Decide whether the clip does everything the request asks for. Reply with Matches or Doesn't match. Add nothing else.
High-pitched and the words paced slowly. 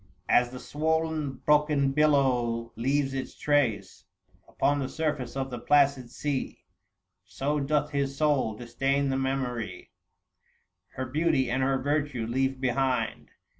Doesn't match